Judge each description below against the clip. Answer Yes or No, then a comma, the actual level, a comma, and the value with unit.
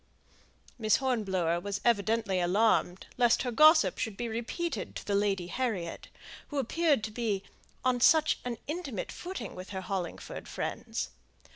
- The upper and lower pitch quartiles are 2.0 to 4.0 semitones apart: No, average, 4.8 semitones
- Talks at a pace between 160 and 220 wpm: No, average, 150 wpm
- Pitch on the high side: Yes, high, 225 Hz